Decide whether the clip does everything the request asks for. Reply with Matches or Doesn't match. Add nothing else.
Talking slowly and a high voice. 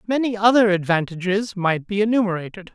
Matches